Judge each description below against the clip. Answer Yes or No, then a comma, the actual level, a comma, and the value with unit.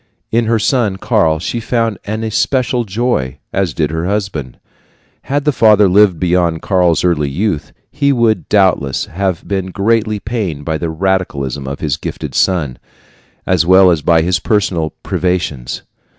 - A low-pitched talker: Yes, very low, 95 Hz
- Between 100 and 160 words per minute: Yes, average, 155 wpm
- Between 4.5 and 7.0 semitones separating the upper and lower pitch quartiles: Yes, average, 5.1 semitones